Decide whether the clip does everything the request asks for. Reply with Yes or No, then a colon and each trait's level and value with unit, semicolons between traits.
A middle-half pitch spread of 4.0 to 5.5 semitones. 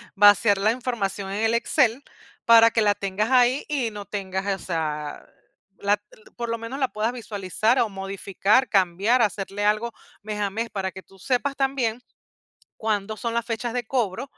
No: average, 3.2 semitones